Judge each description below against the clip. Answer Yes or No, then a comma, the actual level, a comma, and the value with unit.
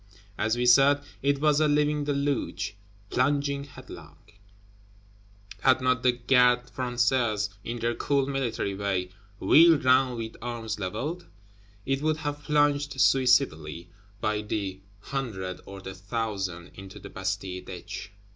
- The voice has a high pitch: No, low, 125 Hz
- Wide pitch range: Yes, wide, 5.8 semitones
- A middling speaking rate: No, slow, 130 wpm